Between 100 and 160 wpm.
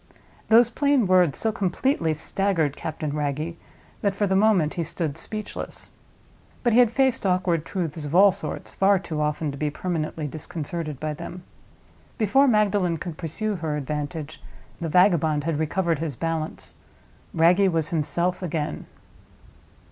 Yes: average, 150 wpm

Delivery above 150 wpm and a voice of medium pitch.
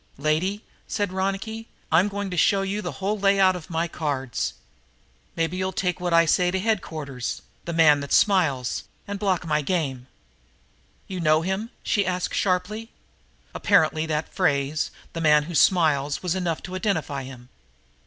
Yes: average, 165 wpm; medium, 175 Hz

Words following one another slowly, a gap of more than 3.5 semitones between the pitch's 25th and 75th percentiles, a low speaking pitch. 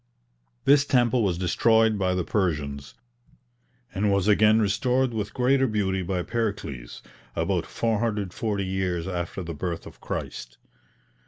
Yes: slow, 130 wpm; average, 4.0 semitones; low, 100 Hz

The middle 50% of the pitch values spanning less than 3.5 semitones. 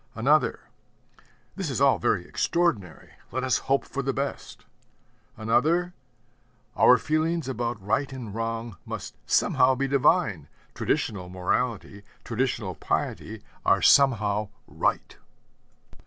No: average, 4.6 semitones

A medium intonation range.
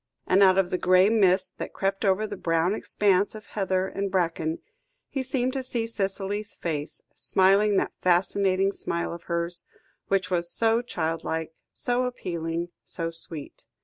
Yes: average, 3.3 semitones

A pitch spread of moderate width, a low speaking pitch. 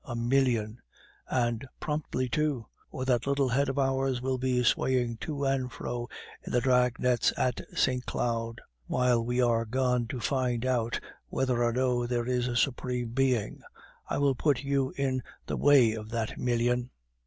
No: narrow, 1.8 semitones; low, 125 Hz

